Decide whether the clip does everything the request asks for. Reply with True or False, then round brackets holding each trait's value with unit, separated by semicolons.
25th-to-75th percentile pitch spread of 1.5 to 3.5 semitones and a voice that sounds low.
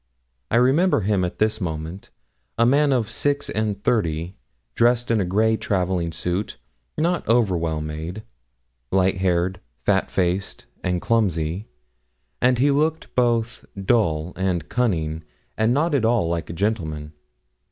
False (5.5 semitones; 100 Hz)